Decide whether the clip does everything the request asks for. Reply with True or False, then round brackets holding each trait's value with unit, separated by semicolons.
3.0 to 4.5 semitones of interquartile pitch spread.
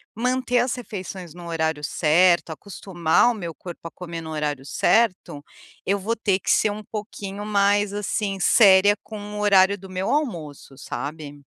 True (3.9 semitones)